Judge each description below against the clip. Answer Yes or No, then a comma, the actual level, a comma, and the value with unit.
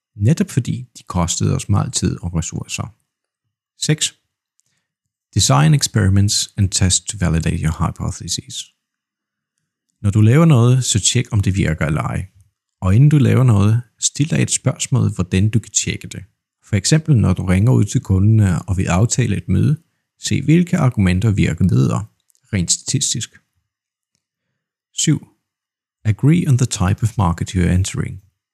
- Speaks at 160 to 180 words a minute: No, average, 150 wpm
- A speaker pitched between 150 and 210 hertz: No, low, 110 Hz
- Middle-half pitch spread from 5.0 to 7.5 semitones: Yes, average, 5.3 semitones